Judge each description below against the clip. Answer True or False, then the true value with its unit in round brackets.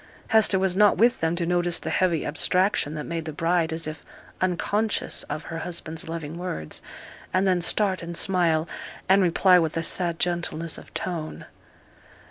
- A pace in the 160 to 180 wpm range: True (170 wpm)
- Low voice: False (170 Hz)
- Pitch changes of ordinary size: False (2.3 semitones)